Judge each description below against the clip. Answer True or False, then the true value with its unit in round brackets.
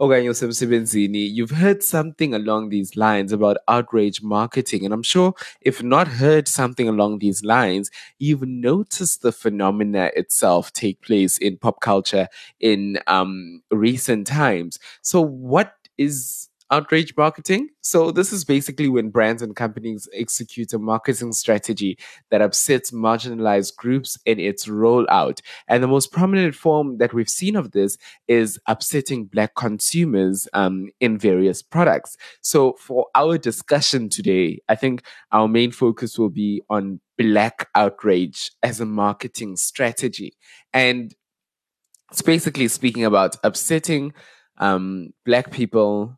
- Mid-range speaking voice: False (115 Hz)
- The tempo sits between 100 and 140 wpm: True (135 wpm)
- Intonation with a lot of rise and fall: False (4.7 semitones)